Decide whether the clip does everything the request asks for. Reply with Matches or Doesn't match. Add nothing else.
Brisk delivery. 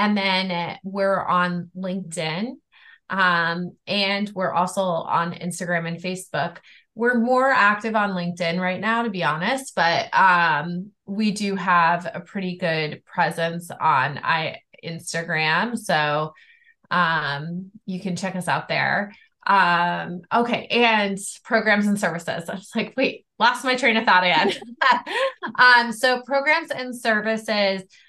Doesn't match